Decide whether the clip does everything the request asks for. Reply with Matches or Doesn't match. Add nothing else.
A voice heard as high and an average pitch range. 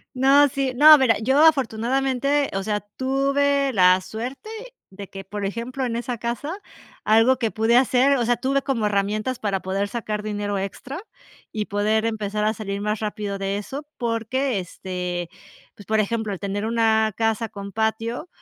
Matches